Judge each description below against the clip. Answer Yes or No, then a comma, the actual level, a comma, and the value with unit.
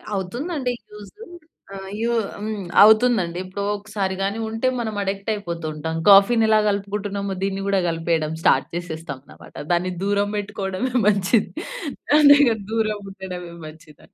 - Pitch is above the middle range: Yes, high, 200 Hz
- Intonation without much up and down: No, average, 3.0 semitones